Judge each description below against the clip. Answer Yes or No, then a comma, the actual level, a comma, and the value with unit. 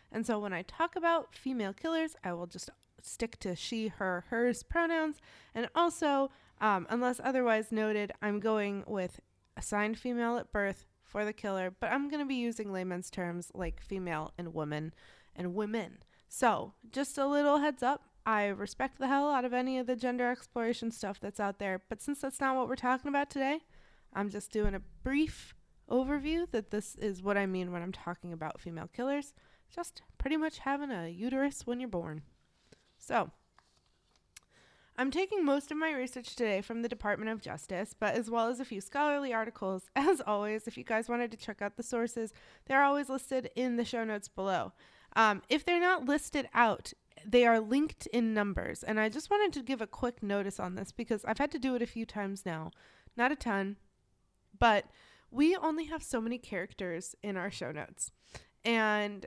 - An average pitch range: Yes, average, 4.9 semitones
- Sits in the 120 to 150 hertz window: No, high, 230 Hz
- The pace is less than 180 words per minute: No, average, 195 wpm